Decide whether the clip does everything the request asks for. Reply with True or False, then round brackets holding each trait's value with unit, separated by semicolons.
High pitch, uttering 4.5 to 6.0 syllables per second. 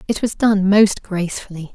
True (195 Hz; 5.0 syllables/s)